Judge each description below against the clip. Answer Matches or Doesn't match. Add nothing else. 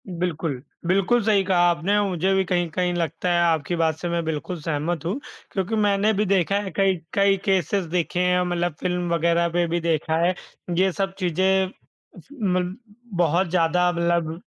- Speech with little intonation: Matches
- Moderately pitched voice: Matches